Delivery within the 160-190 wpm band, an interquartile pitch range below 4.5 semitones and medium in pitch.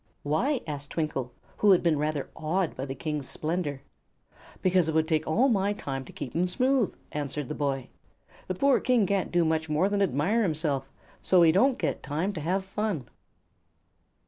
No: average, 185 wpm; average, 4.9 semitones; medium, 160 Hz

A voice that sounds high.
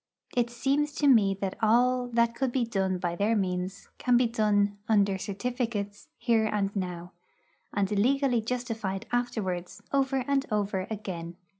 Yes: high, 220 Hz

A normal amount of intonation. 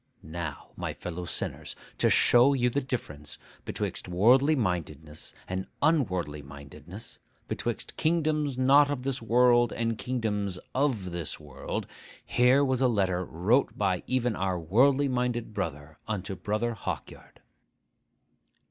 No: wide, 6.4 semitones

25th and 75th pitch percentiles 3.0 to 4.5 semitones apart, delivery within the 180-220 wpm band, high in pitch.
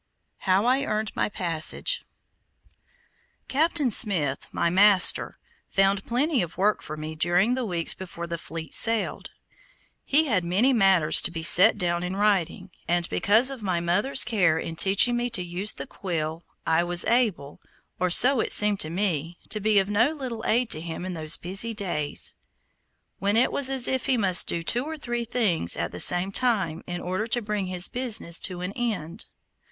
No: average, 5.2 semitones; average, 185 wpm; high, 195 Hz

